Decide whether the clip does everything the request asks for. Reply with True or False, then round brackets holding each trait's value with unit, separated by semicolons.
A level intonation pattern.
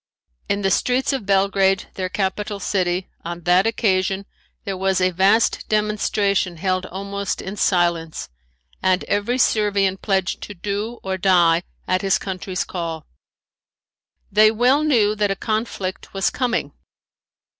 True (2.2 semitones)